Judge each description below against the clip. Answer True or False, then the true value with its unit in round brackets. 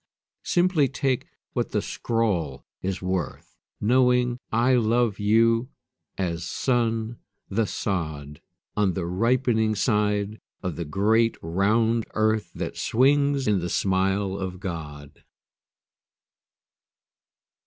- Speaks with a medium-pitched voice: False (105 Hz)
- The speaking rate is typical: False (105 wpm)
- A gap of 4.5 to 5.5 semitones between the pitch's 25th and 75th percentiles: False (4.1 semitones)